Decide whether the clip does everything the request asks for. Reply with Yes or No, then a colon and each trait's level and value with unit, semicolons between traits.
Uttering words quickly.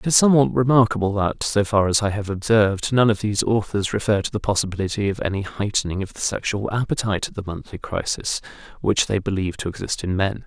Yes: fast, 210 wpm